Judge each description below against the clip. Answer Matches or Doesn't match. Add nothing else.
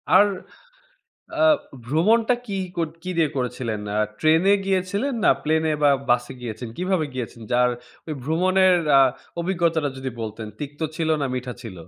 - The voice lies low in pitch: Doesn't match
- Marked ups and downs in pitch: Matches